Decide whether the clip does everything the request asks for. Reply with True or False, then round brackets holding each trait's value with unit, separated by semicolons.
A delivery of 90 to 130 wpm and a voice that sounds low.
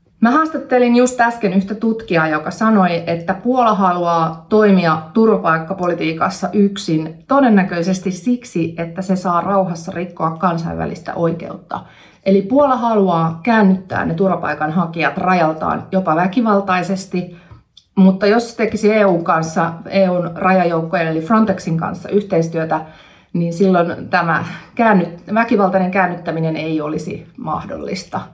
False (110 wpm; 185 Hz)